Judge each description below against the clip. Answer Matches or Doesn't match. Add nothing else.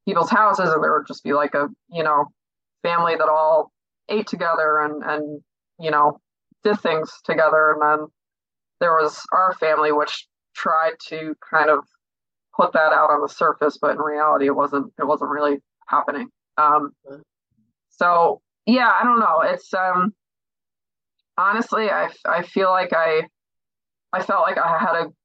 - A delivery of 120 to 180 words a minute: Matches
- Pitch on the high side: Doesn't match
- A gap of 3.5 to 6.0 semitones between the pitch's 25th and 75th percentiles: Doesn't match